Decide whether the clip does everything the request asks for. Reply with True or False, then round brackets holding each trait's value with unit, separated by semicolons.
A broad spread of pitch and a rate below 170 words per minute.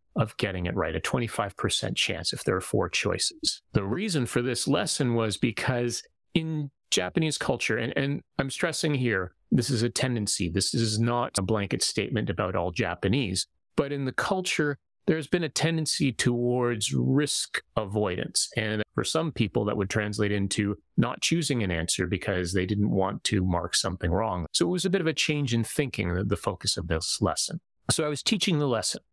False (6.3 semitones; 190 wpm)